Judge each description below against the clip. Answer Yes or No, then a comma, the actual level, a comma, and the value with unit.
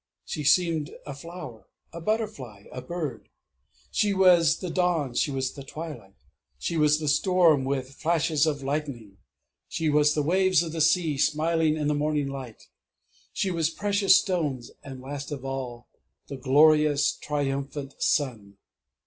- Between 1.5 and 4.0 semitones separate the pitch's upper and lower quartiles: Yes, average, 3.6 semitones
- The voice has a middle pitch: Yes, medium, 150 Hz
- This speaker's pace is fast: No, average, 150 wpm